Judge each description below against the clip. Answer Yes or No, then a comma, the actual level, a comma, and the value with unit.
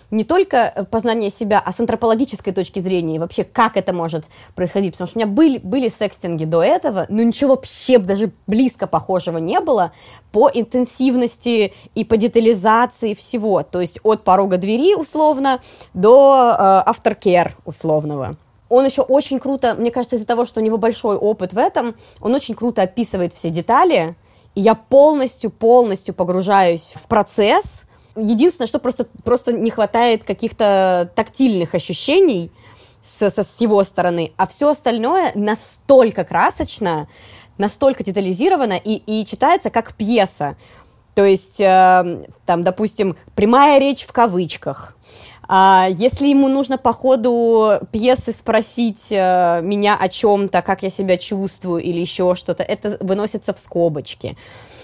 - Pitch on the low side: No, high, 210 Hz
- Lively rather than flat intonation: No, average, 4.5 semitones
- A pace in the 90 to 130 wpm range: No, average, 145 wpm